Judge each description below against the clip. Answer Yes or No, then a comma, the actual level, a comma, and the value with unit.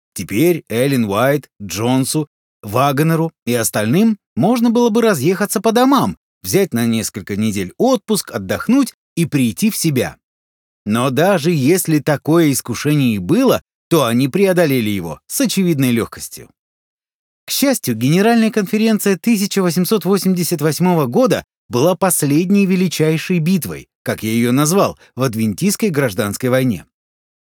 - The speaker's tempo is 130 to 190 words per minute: No, average, 120 wpm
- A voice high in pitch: No, medium, 160 Hz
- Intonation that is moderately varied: No, wide, 8.2 semitones